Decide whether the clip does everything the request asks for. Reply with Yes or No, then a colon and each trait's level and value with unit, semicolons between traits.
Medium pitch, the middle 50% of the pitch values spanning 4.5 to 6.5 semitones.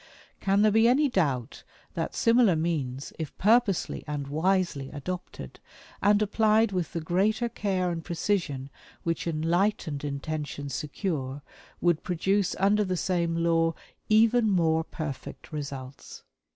Yes: medium, 170 Hz; average, 5.2 semitones